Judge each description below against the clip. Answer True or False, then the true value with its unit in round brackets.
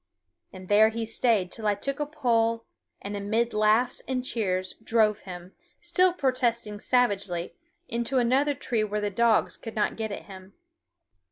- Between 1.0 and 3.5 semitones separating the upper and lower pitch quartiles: True (3.1 semitones)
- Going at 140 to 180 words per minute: True (160 wpm)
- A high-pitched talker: True (225 Hz)